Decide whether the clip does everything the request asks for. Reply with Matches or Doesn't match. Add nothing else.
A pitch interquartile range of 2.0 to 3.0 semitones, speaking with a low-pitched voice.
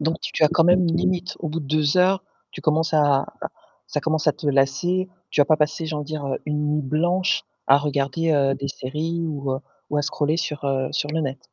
Doesn't match